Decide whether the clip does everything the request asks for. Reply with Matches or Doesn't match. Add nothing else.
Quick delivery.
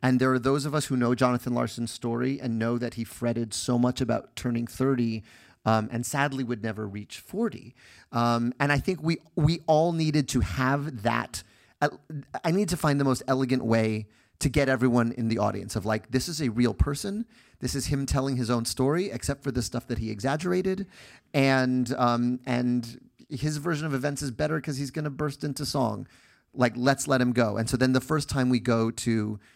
Matches